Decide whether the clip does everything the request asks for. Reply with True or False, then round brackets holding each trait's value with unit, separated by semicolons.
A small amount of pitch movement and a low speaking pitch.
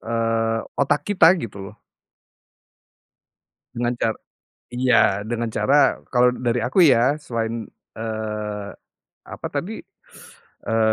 True (2.0 semitones; 115 Hz)